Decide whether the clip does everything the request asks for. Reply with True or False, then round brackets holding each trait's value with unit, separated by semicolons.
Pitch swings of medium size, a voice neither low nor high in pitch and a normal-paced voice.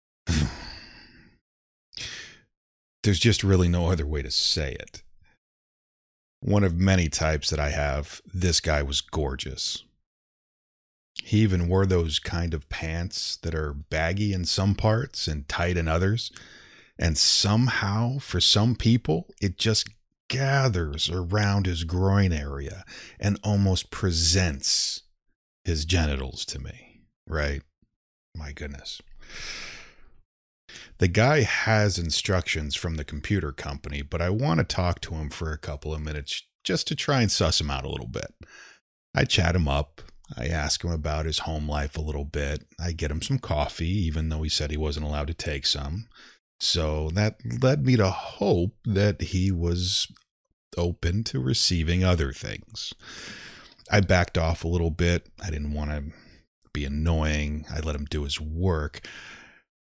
False (4.5 semitones; 85 Hz; 150 wpm)